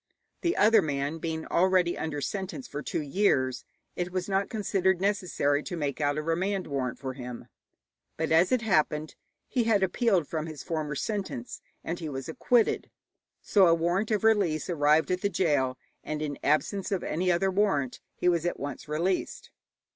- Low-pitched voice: No, medium, 170 Hz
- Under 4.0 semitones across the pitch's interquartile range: No, average, 4.5 semitones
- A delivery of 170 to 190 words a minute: Yes, average, 175 wpm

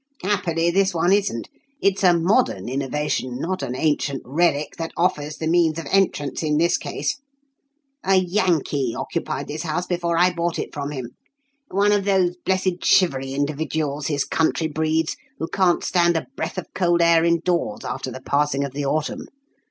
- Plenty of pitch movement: No, average, 3.7 semitones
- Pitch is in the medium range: Yes, medium, 165 Hz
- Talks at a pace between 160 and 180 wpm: Yes, average, 170 wpm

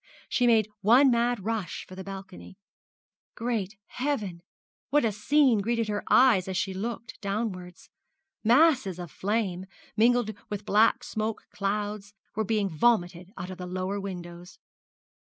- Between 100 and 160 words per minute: Yes, average, 140 wpm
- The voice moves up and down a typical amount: Yes, average, 3.5 semitones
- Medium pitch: No, high, 210 Hz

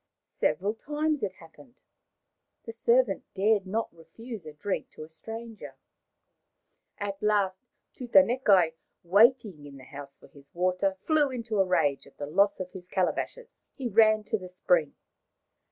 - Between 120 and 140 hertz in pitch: No, high, 200 Hz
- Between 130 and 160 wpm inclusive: Yes, average, 150 wpm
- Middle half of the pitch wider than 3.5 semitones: Yes, average, 4.4 semitones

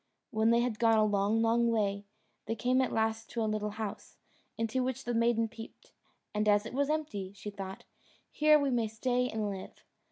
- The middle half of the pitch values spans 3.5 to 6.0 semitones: No, narrow, 2.5 semitones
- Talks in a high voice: Yes, high, 225 Hz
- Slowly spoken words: No, average, 200 wpm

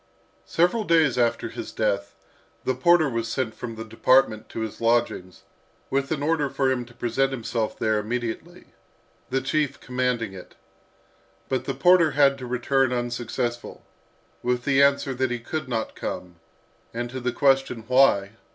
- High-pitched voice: No, low, 125 Hz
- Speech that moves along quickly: No, average, 160 wpm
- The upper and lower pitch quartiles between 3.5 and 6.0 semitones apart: No, average, 3.0 semitones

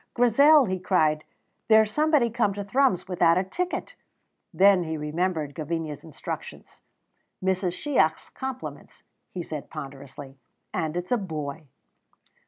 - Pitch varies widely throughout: Yes, wide, 6.1 semitones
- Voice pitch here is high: No, medium, 180 Hz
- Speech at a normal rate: No, slow, 125 wpm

